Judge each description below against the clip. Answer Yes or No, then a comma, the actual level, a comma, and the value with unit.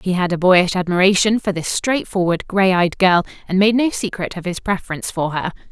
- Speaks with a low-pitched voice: No, medium, 185 Hz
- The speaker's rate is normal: No, fast, 210 wpm